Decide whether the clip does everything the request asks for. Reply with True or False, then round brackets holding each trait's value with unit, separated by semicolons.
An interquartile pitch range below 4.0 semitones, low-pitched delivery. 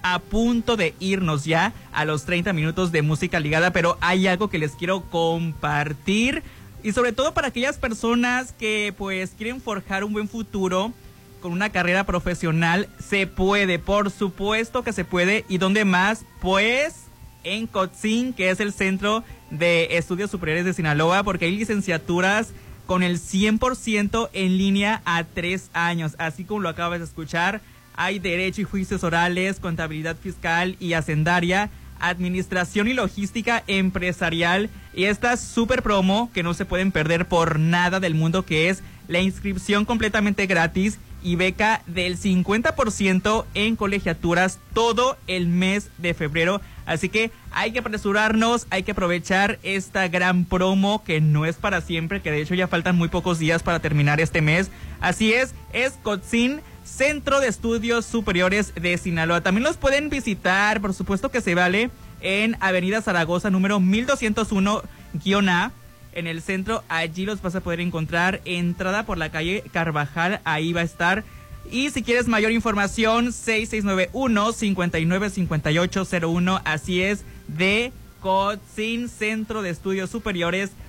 False (3.6 semitones; 190 Hz)